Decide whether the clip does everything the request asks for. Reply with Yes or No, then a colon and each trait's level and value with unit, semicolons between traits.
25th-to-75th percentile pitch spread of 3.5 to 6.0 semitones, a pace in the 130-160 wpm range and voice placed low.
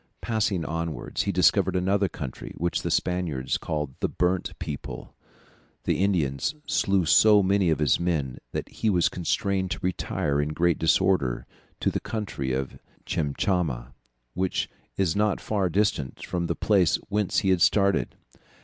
Yes: average, 4.5 semitones; average, 150 wpm; very low, 90 Hz